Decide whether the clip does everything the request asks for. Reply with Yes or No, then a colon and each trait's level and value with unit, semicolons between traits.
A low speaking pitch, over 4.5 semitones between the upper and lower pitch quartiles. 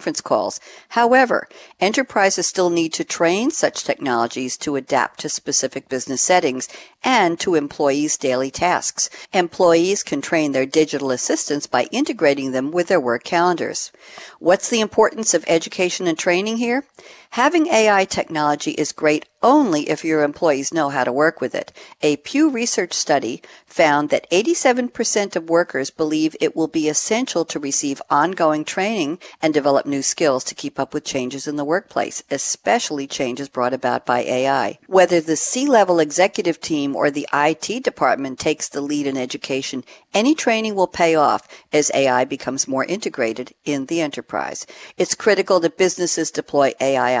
No: medium, 155 Hz; wide, 5.5 semitones